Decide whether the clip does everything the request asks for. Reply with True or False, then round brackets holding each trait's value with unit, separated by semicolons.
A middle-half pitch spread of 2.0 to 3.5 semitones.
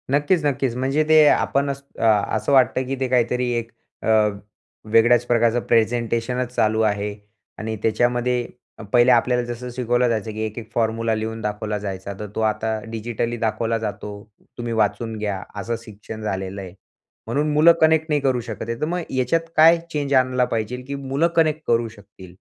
True (2.9 semitones)